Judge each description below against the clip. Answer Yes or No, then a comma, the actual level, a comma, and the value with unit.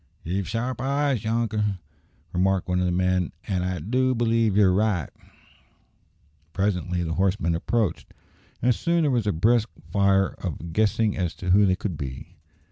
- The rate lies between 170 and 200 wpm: No, average, 160 wpm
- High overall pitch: No, low, 100 Hz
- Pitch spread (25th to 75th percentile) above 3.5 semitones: Yes, average, 4.0 semitones